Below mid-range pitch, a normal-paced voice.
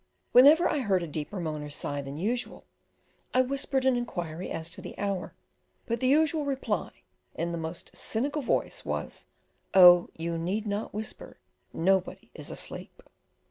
No: high, 200 Hz; average, 160 wpm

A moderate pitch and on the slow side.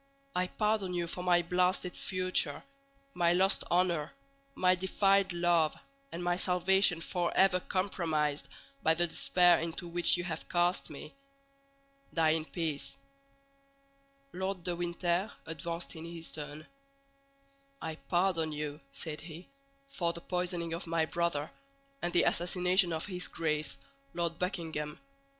Yes: medium, 175 Hz; slow, 130 wpm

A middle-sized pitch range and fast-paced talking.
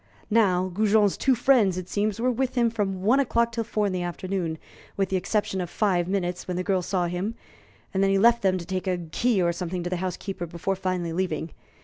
Yes: average, 3.2 semitones; fast, 230 wpm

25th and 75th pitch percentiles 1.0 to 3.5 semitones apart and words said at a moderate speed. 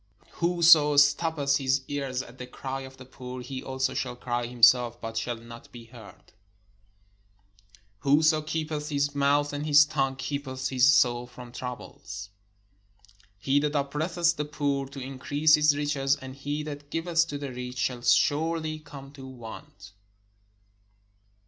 Yes: average, 2.8 semitones; average, 150 wpm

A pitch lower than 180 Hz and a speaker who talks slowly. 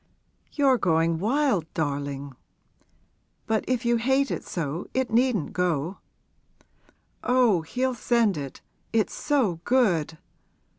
No: high, 210 Hz; slow, 110 wpm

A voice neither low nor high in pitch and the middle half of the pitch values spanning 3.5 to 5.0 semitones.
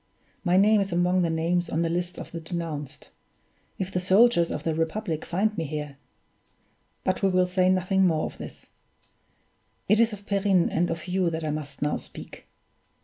No: medium, 175 Hz; average, 2.7 semitones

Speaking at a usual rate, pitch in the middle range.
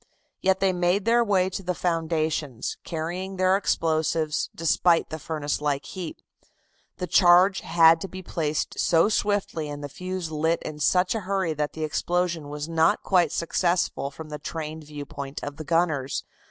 Yes: average, 165 wpm; medium, 165 Hz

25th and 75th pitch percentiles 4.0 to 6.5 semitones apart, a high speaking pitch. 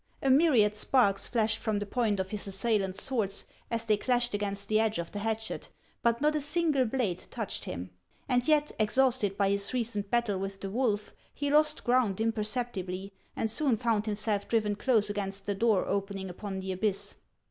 No: average, 3.4 semitones; high, 215 Hz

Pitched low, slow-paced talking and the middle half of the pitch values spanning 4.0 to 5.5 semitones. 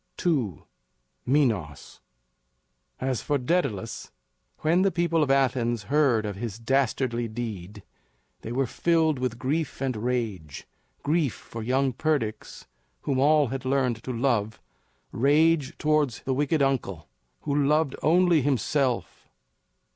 Yes: low, 130 Hz; slow, 125 wpm; average, 4.5 semitones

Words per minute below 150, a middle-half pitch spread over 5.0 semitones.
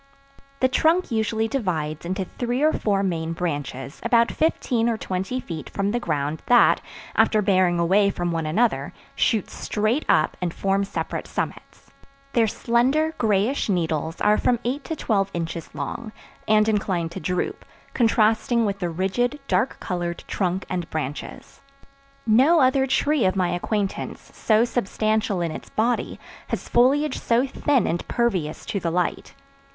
No: average, 155 wpm; wide, 5.4 semitones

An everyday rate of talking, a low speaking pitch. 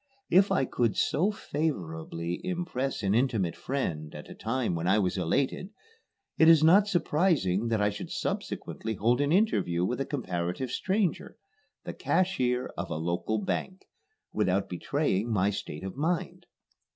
Yes: average, 150 wpm; low, 120 Hz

